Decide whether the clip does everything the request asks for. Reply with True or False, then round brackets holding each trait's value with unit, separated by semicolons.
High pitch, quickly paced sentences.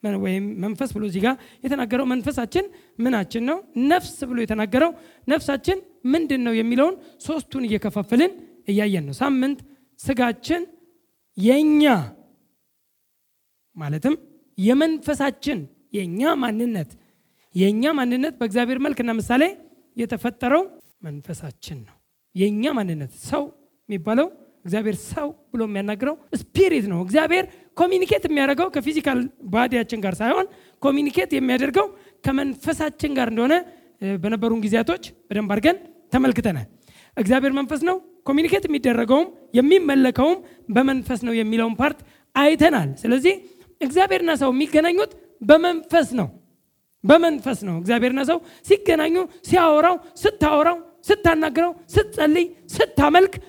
False (280 Hz; 100 wpm)